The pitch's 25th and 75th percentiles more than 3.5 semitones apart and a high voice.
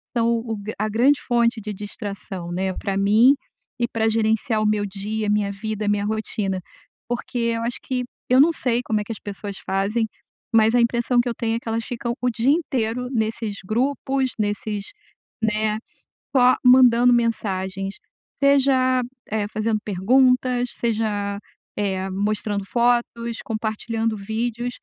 No: average, 2.7 semitones; high, 225 Hz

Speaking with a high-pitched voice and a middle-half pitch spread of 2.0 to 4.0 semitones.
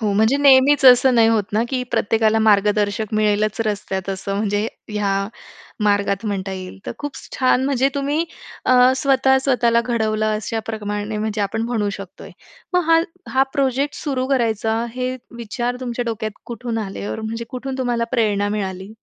Yes: high, 225 Hz; average, 3.6 semitones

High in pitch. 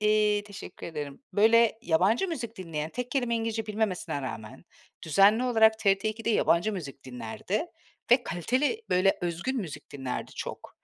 Yes: high, 210 Hz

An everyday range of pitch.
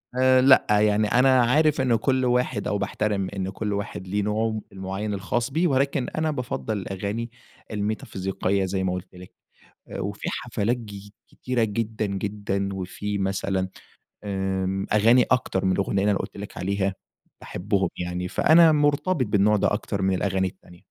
Yes: average, 3.9 semitones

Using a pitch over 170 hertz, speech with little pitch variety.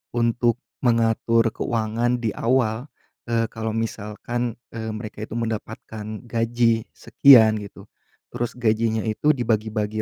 No: low, 115 Hz; narrow, 1.4 semitones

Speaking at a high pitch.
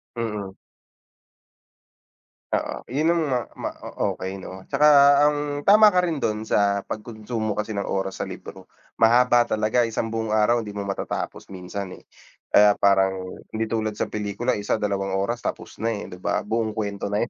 No: low, 110 Hz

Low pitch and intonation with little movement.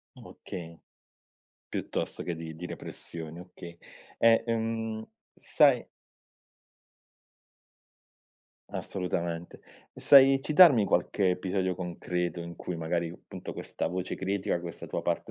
No: very low, 90 Hz; average, 4.0 semitones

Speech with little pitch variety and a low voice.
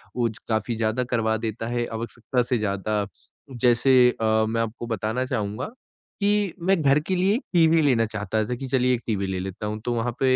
No: average, 3.0 semitones; low, 120 Hz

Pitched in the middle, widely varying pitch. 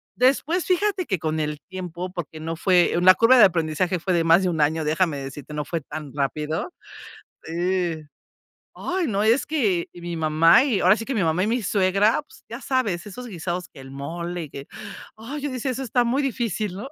Yes: medium, 180 Hz; wide, 6.4 semitones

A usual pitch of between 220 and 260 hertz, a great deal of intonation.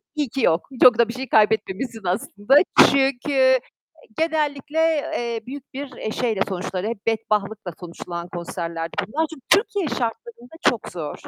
Yes: high, 235 Hz; wide, 5.8 semitones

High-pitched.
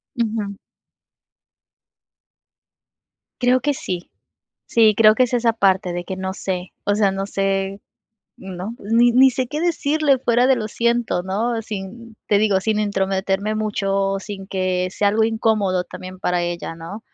Yes: high, 205 Hz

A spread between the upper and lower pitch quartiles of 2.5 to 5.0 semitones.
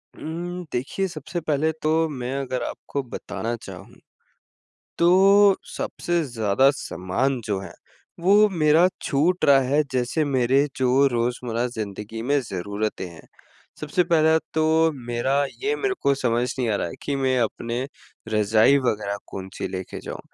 No: wide, 5.4 semitones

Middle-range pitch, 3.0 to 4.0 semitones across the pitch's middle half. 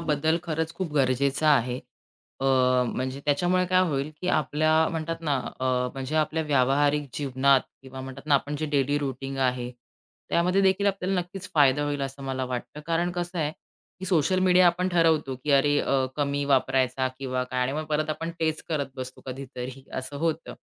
Yes: medium, 145 Hz; average, 3.6 semitones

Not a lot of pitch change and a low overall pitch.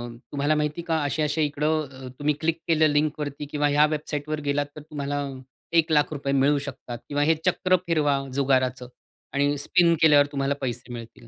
No: narrow, 1.7 semitones; medium, 145 Hz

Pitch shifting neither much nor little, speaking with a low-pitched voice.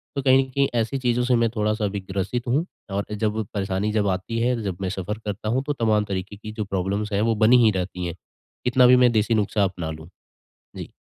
Yes: average, 3.5 semitones; low, 105 Hz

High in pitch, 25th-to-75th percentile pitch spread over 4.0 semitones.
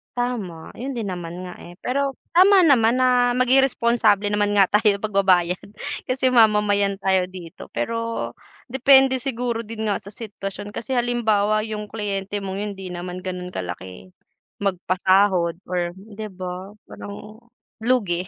Yes: high, 205 Hz; average, 4.5 semitones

